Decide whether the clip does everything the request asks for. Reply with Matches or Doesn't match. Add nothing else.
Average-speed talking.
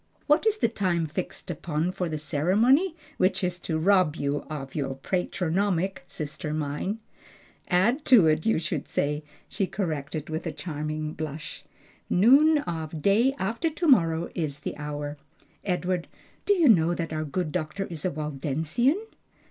Matches